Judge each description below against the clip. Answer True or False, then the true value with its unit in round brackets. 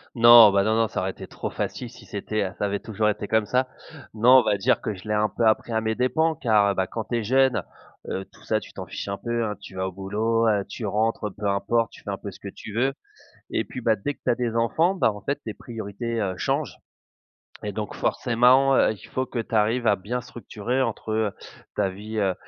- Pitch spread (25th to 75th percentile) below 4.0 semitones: True (2.8 semitones)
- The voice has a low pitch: True (110 Hz)